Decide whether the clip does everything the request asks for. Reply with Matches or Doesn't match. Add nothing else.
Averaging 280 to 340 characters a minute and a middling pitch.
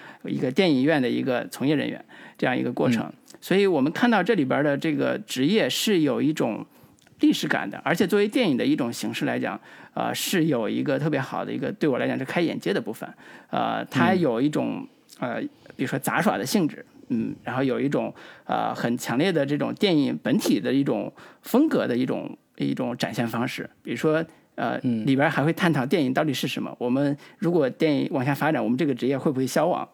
Matches